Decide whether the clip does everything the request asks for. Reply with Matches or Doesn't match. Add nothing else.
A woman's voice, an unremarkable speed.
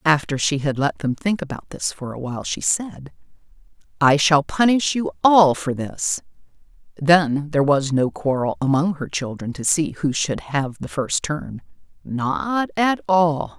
Matches